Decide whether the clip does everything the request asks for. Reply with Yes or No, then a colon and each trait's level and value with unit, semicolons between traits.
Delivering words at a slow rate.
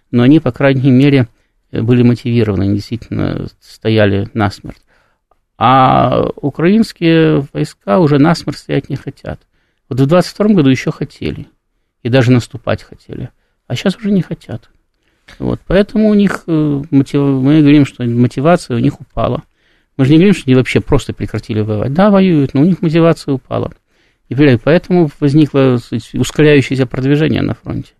No: average, 150 wpm